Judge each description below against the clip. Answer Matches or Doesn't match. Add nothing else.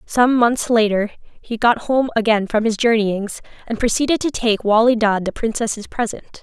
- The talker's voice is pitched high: Matches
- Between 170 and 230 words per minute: Matches